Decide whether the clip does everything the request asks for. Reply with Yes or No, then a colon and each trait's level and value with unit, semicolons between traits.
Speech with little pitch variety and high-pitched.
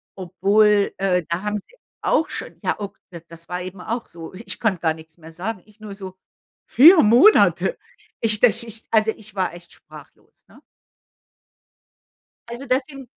No: average, 4.1 semitones; high, 205 Hz